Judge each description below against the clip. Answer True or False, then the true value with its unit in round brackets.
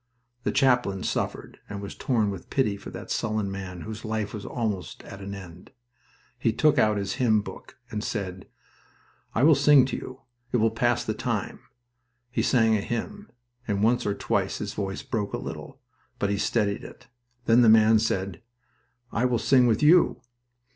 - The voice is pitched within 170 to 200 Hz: False (110 Hz)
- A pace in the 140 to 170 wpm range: False (180 wpm)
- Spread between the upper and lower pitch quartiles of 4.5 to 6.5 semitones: False (3.7 semitones)